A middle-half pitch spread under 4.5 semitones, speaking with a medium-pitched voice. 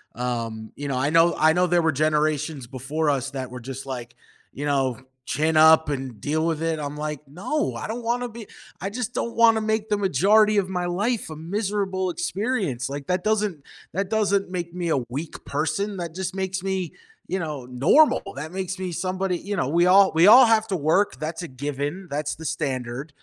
No: average, 5.2 semitones; medium, 165 Hz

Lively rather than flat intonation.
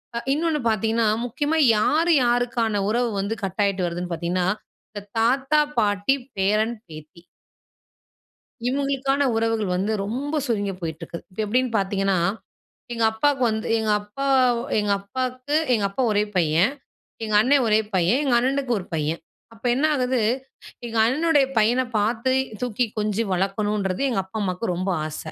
No: average, 4.5 semitones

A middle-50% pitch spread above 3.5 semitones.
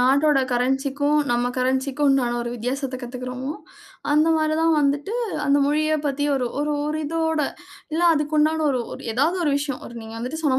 No: average, 3.2 semitones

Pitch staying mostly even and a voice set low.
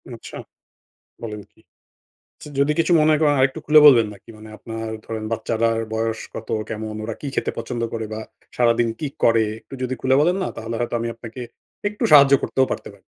No: average, 3.4 semitones; low, 115 Hz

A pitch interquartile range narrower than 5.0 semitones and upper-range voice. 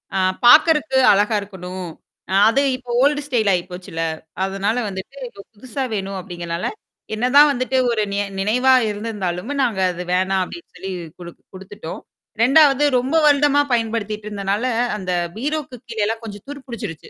No: wide, 5.4 semitones; high, 215 Hz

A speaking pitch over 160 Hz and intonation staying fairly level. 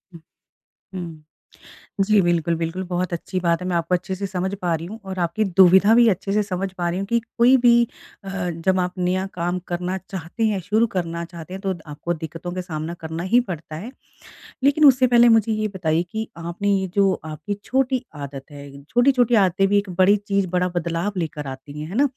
No: medium, 185 Hz; average, 3.4 semitones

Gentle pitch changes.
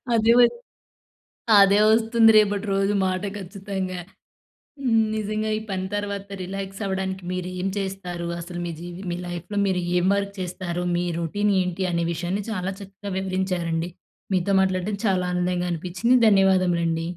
Yes: narrow, 2.2 semitones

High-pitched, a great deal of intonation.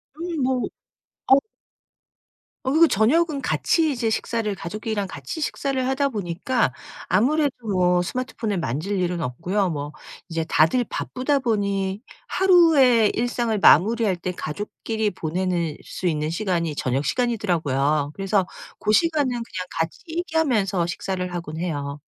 Yes: high, 205 Hz; wide, 6.7 semitones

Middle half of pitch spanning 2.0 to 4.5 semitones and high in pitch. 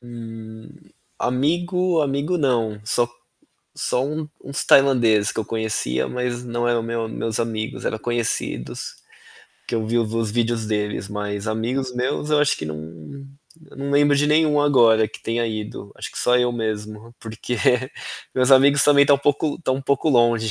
No: average, 3.9 semitones; low, 120 Hz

